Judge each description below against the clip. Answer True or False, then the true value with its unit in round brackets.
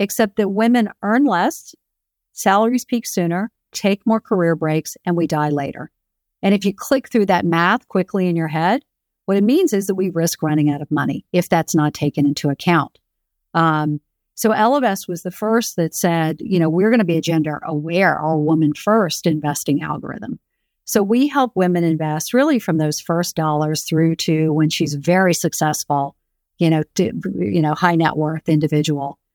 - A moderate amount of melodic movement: True (4.5 semitones)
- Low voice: False (170 Hz)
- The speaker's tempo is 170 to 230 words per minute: True (185 wpm)